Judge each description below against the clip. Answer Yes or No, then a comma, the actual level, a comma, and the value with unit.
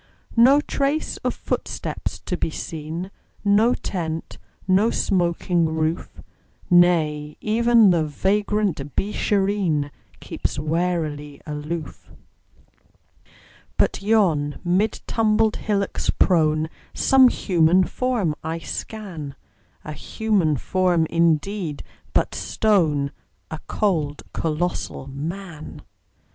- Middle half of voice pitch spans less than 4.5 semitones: No, average, 4.8 semitones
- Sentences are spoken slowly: Yes, slow, 95 wpm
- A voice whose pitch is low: No, medium, 175 Hz